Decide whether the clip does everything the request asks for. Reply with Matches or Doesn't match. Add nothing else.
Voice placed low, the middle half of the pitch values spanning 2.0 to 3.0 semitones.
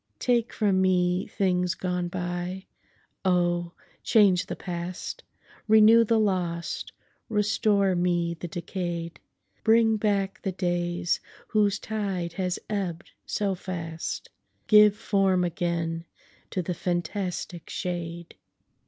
Doesn't match